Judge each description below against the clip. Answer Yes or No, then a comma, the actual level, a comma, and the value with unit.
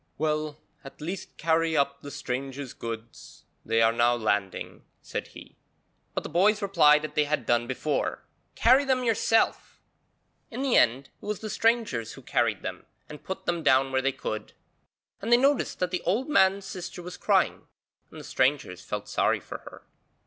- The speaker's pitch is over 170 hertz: No, medium, 155 Hz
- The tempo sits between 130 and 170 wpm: No, average, 180 wpm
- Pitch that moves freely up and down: Yes, wide, 7.1 semitones